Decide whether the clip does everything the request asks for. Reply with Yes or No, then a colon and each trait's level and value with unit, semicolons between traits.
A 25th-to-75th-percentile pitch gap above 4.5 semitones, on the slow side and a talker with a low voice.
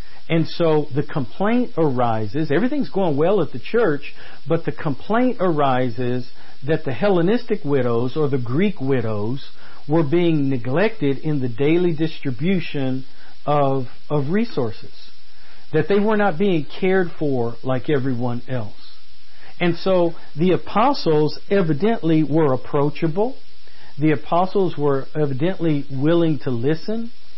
No: average, 4.9 semitones; slow, 125 wpm; medium, 155 Hz